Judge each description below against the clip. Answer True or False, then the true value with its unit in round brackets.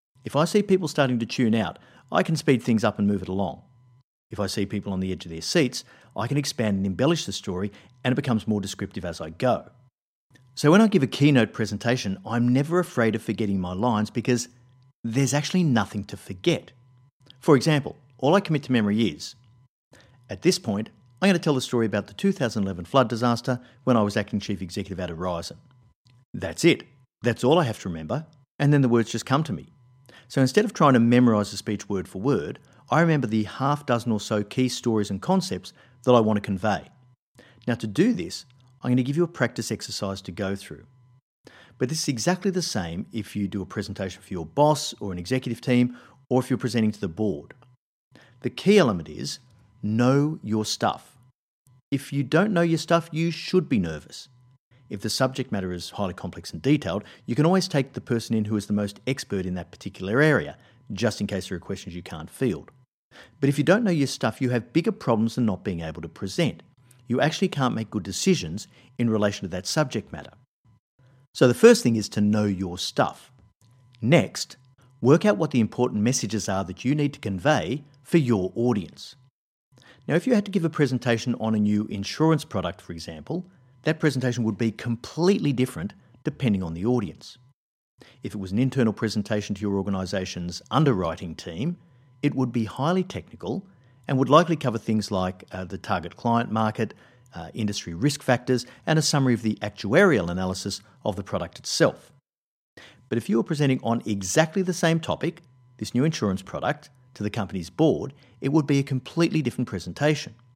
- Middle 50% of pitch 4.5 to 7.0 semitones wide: True (5.2 semitones)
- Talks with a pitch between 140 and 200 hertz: False (125 Hz)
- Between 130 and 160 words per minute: False (200 wpm)